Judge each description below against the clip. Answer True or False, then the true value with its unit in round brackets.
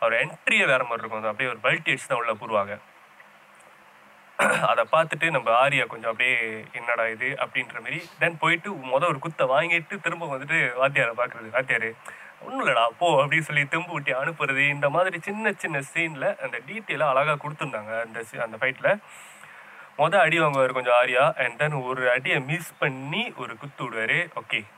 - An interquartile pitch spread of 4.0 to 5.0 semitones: True (4.7 semitones)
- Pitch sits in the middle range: True (145 Hz)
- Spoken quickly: True (165 wpm)